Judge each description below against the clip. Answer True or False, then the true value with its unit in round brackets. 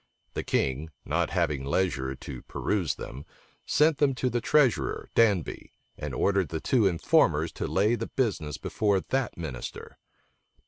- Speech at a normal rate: True (145 wpm)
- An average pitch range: False (8.3 semitones)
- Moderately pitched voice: False (95 Hz)